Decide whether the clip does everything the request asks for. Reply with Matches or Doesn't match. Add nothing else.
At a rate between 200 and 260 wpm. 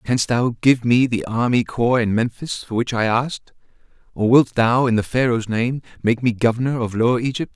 Matches